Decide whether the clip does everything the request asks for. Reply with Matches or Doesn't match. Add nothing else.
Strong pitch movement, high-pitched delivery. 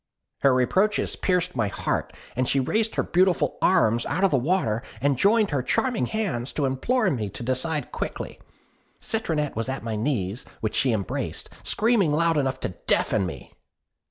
Doesn't match